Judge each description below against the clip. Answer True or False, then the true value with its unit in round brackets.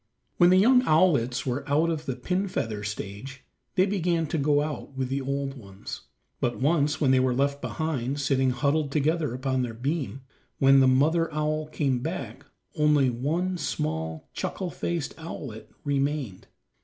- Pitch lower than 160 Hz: True (140 Hz)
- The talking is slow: False (165 wpm)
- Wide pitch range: False (3.5 semitones)